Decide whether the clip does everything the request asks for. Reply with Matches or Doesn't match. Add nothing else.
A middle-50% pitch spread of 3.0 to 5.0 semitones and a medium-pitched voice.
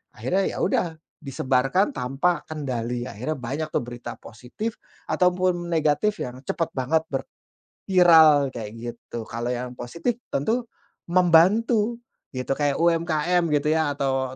Doesn't match